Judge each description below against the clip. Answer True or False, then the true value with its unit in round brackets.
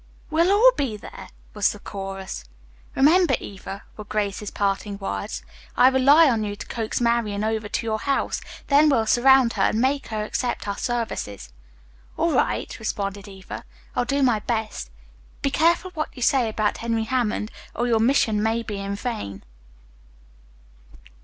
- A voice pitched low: False (225 Hz)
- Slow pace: False (160 wpm)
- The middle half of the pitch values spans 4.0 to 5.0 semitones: True (4.3 semitones)